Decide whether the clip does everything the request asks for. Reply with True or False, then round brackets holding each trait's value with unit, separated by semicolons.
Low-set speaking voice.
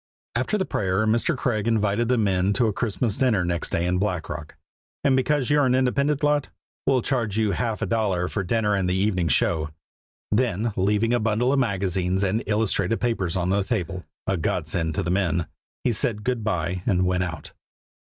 True (105 Hz)